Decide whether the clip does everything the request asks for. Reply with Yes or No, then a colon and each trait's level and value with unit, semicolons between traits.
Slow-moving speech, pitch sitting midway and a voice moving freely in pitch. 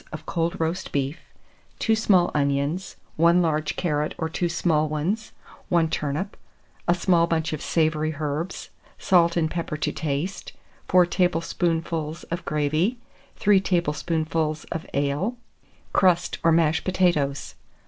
No: slow, 130 wpm; medium, 165 Hz; narrow, 2.5 semitones